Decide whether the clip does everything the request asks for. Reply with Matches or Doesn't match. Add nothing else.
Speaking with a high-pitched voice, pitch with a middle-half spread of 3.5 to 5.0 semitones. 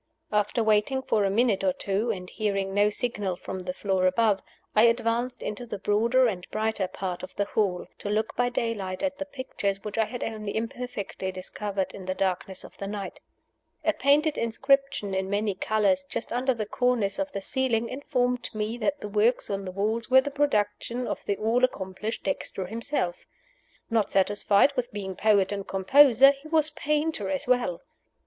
Matches